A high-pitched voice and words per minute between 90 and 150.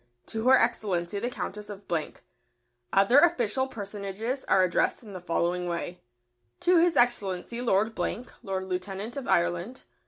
Yes: high, 205 Hz; average, 145 wpm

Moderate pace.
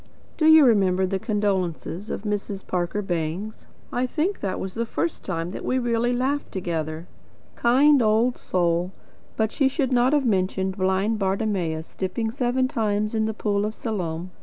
Yes: average, 160 wpm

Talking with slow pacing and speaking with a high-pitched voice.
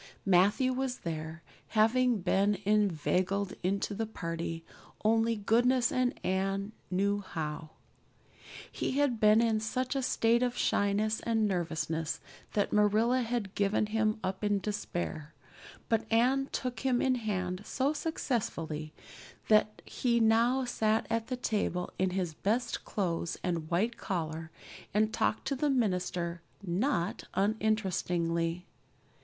Yes: slow, 130 wpm; high, 210 Hz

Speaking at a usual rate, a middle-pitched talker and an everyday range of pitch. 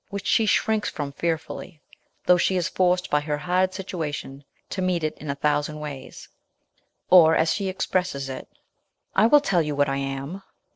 Yes: average, 190 wpm; medium, 165 Hz; average, 4.1 semitones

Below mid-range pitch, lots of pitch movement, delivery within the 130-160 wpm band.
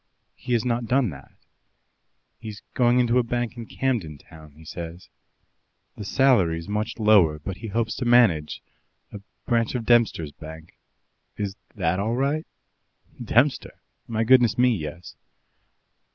Yes: low, 110 Hz; wide, 6.1 semitones; average, 140 wpm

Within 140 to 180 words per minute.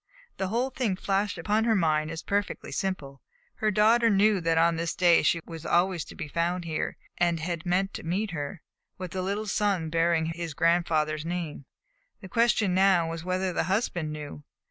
No: average, 190 wpm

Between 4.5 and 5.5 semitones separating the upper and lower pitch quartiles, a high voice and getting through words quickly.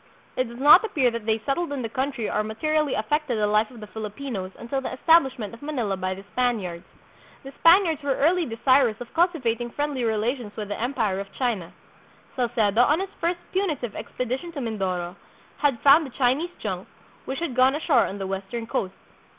No: average, 5.0 semitones; high, 245 Hz; average, 190 wpm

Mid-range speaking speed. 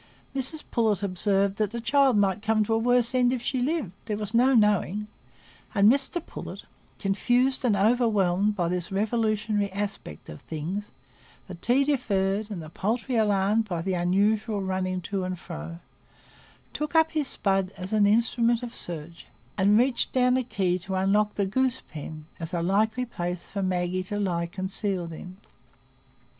Yes: average, 165 wpm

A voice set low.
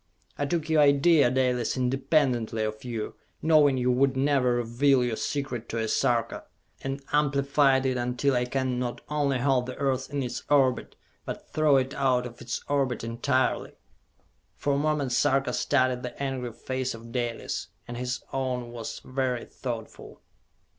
Yes: low, 130 Hz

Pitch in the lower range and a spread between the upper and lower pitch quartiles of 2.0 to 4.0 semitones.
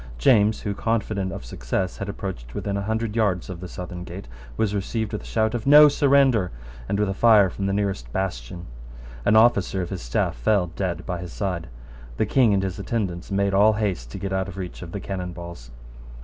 Yes: very low, 95 Hz; average, 3.2 semitones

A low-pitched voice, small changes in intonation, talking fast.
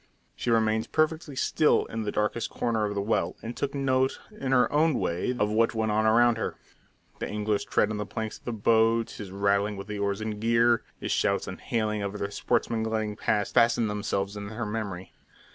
Yes: low, 110 Hz; narrow, 2.1 semitones; fast, 210 wpm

